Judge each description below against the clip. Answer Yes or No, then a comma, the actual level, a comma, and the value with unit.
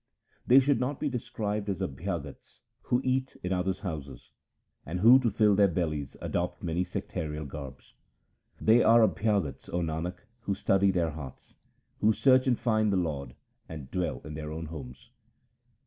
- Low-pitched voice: Yes, very low, 90 Hz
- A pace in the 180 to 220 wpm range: No, average, 165 wpm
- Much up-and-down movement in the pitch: Yes, wide, 5.9 semitones